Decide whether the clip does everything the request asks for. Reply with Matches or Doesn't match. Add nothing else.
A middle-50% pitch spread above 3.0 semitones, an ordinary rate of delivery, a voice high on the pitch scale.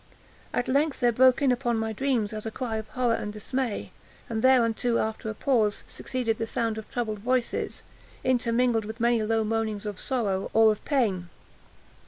Doesn't match